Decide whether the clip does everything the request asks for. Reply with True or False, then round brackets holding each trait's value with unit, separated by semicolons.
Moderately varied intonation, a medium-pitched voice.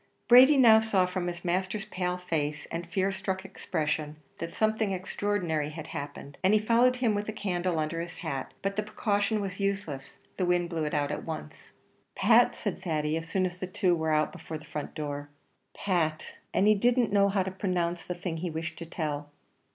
True (4.2 semitones; 180 Hz)